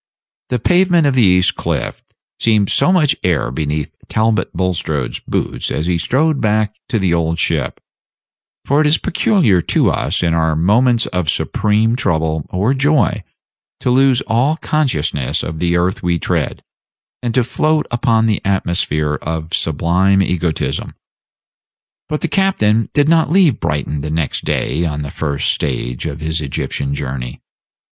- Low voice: Yes, very low, 90 Hz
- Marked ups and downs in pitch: Yes, wide, 7.9 semitones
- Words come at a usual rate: Yes, average, 155 wpm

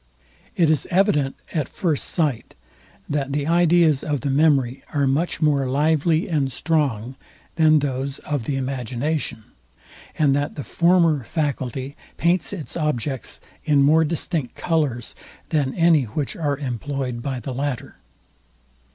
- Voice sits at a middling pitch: Yes, medium, 145 Hz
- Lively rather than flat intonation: No, average, 3.1 semitones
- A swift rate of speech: No, slow, 135 wpm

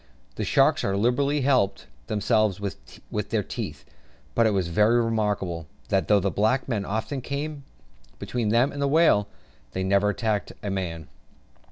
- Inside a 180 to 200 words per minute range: No, average, 160 wpm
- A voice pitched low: Yes, low, 105 Hz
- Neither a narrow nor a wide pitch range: Yes, average, 3.8 semitones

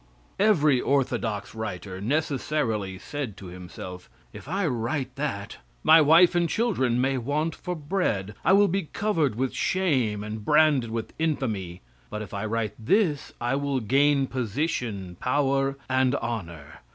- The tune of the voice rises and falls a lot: Yes, wide, 6.1 semitones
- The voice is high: No, low, 130 Hz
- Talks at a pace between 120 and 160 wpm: Yes, average, 145 wpm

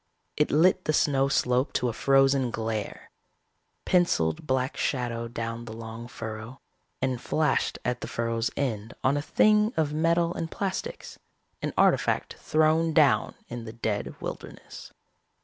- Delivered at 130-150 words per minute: Yes, average, 145 wpm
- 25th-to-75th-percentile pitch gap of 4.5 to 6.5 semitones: Yes, average, 5.1 semitones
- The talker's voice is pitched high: No, low, 130 Hz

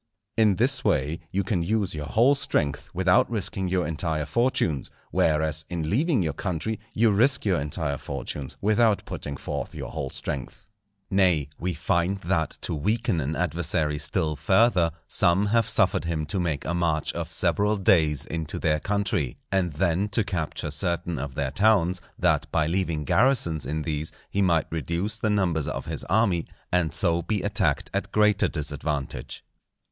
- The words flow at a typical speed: Yes, average, 165 wpm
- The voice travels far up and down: No, average, 4.7 semitones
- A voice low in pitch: Yes, very low, 85 Hz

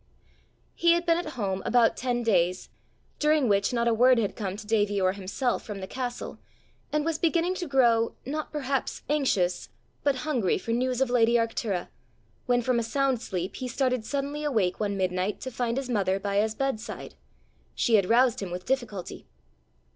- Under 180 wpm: No, average, 185 wpm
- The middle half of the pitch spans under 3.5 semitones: No, average, 4.8 semitones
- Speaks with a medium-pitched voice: No, high, 235 Hz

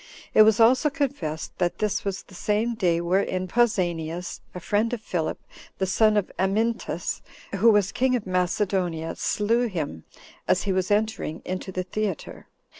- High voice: Yes, high, 195 Hz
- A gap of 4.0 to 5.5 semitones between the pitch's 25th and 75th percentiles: No, average, 3.4 semitones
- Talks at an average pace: Yes, average, 160 wpm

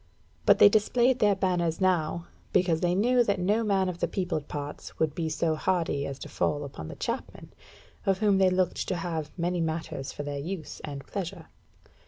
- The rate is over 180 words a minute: Yes, average, 195 wpm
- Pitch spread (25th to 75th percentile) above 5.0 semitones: No, average, 3.6 semitones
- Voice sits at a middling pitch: Yes, medium, 175 Hz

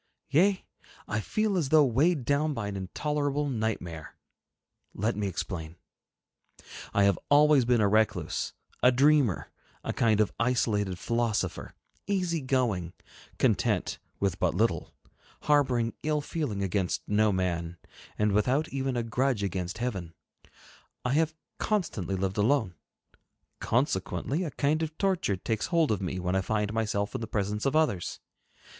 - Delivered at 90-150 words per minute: Yes, average, 145 wpm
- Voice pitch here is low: Yes, low, 115 Hz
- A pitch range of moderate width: No, wide, 6.6 semitones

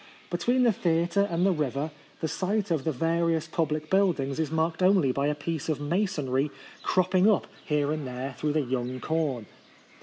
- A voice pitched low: No, medium, 160 Hz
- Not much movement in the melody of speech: No, average, 3.8 semitones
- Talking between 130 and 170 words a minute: No, average, 185 wpm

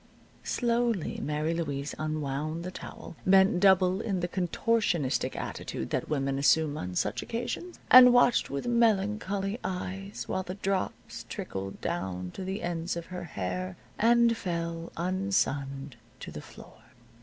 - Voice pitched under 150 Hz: No, medium, 180 Hz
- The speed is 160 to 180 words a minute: No, average, 140 wpm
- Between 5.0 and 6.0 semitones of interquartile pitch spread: Yes, wide, 5.6 semitones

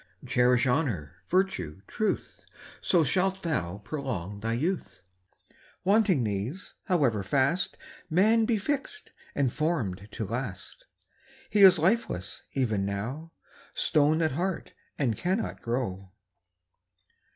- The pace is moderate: No, slow, 110 wpm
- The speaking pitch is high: No, medium, 140 Hz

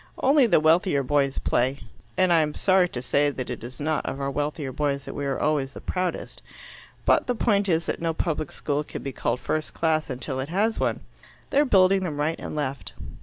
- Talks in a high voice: No, medium, 150 Hz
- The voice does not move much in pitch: No, average, 4.5 semitones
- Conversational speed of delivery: No, fast, 220 wpm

